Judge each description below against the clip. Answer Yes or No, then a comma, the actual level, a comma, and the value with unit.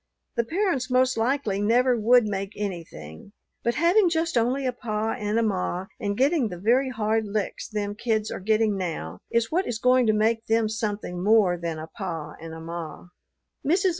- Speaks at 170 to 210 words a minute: Yes, average, 185 wpm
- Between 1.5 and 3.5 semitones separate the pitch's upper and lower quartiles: No, average, 4.1 semitones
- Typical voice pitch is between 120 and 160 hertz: No, high, 220 Hz